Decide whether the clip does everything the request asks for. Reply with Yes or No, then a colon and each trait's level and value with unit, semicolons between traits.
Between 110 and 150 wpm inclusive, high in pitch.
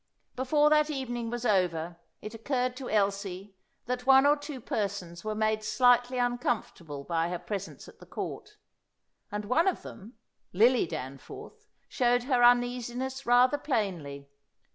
Yes: average, 140 wpm; high, 235 Hz